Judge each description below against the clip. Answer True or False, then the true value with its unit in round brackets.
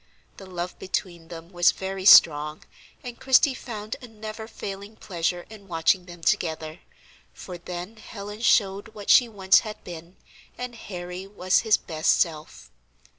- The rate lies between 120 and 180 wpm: True (150 wpm)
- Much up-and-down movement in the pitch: False (3.6 semitones)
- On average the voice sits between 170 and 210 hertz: True (190 Hz)